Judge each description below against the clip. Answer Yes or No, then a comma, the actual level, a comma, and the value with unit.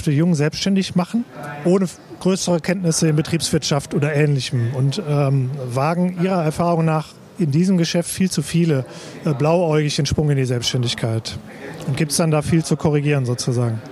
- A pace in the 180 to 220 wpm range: No, average, 170 wpm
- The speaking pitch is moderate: Yes, medium, 155 Hz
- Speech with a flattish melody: No, average, 3.5 semitones